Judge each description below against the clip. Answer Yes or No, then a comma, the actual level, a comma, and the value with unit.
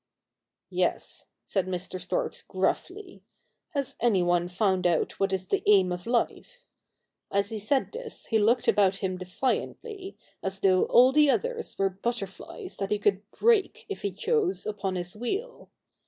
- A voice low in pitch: No, high, 210 Hz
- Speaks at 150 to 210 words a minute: Yes, average, 170 wpm